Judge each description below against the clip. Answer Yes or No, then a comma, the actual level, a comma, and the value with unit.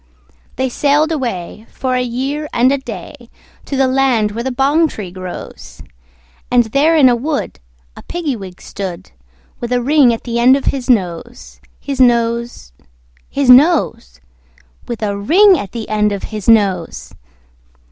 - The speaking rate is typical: Yes, average, 160 wpm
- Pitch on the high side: Yes, high, 245 Hz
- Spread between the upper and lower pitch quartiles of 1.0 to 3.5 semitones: No, average, 4.5 semitones